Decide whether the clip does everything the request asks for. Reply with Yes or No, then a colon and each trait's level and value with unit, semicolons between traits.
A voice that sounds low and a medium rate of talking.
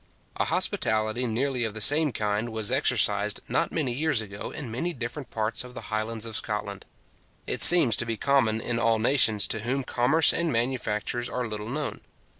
Yes: low, 115 Hz; average, 185 wpm